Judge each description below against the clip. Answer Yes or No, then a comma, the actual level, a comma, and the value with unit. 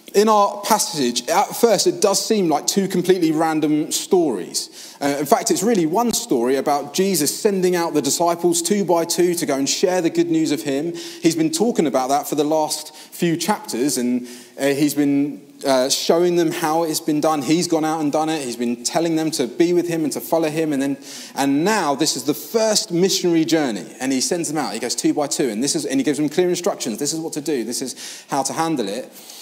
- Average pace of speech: No, fast, 240 wpm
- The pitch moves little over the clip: No, average, 4.0 semitones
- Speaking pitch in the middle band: Yes, medium, 160 Hz